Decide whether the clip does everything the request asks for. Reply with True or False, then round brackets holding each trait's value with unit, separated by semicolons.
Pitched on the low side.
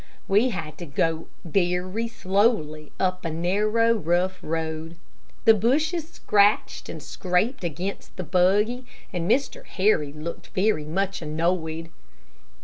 False (185 Hz)